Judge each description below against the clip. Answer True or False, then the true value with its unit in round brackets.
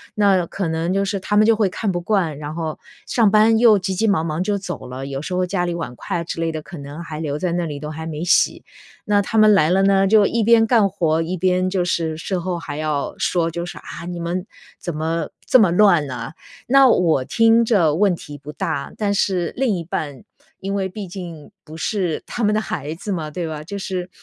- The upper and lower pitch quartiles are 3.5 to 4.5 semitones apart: True (4.1 semitones)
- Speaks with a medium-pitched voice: True (175 Hz)